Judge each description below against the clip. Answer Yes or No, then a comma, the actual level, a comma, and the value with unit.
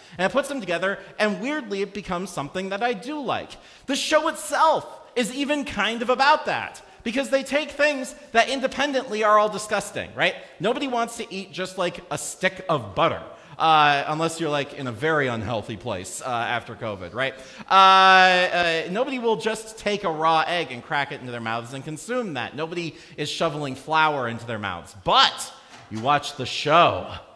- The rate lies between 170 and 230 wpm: Yes, average, 190 wpm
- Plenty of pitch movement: Yes, wide, 7.9 semitones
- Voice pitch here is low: No, medium, 185 Hz